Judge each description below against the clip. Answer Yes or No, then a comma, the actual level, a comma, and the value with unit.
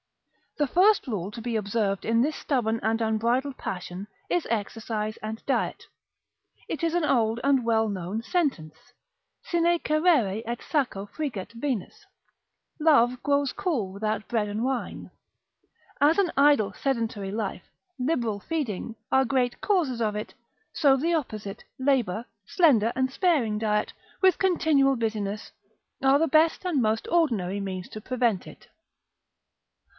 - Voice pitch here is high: Yes, high, 235 Hz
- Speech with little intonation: No, average, 5.2 semitones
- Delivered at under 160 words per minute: Yes, average, 140 wpm